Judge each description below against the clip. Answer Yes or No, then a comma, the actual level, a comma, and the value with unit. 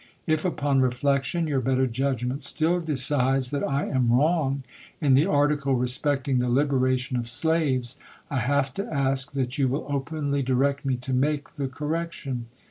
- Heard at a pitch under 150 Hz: Yes, low, 135 Hz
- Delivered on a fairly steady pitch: Yes, narrow, 2.2 semitones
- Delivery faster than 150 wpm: Yes, average, 160 wpm